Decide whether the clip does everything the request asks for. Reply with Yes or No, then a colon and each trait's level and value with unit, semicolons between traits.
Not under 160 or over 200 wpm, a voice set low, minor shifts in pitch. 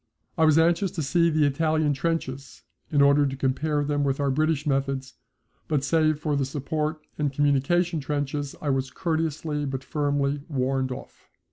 No: average, 165 wpm; medium, 145 Hz; narrow, 2.3 semitones